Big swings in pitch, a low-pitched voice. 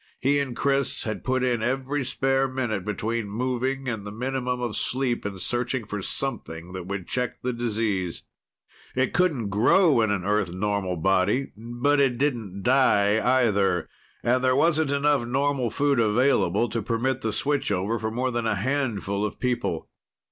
No: average, 4.3 semitones; low, 120 Hz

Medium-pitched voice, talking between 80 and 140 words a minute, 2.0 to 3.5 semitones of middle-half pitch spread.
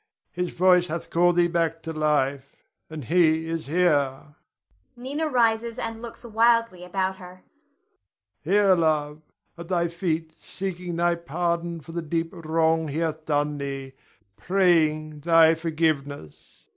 Yes: medium, 165 Hz; slow, 135 wpm; narrow, 2.6 semitones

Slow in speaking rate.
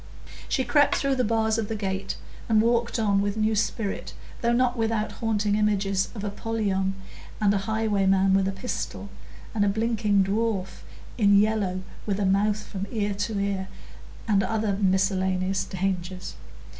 No: average, 155 wpm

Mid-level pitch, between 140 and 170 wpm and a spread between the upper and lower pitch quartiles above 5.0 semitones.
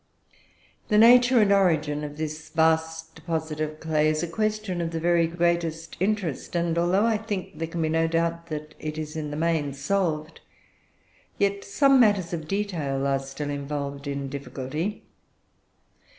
No: medium, 165 Hz; average, 165 wpm; average, 3.4 semitones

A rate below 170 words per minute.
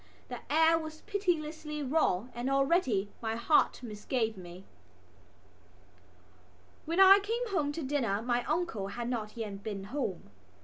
Yes: slow, 135 wpm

